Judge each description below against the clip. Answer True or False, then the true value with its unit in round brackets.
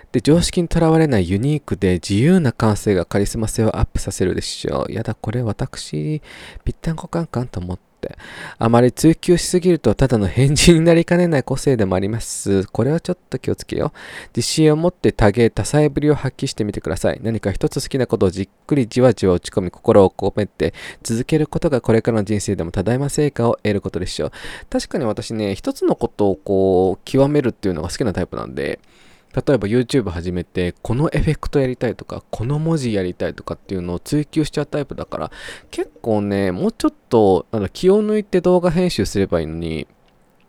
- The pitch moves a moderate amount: False (7.2 semitones)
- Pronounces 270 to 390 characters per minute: False (425 characters per minute)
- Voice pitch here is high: False (120 Hz)